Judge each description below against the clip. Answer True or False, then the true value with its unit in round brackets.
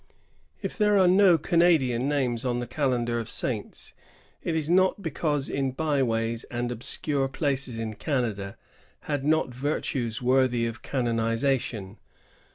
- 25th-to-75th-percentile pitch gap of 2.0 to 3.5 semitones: False (4.3 semitones)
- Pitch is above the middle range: False (130 Hz)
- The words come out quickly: False (135 wpm)